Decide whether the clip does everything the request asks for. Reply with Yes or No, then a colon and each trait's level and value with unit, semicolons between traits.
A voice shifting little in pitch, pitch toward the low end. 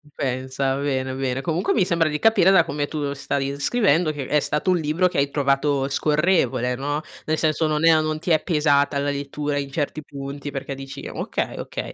No: narrow, 2.2 semitones; medium, 145 Hz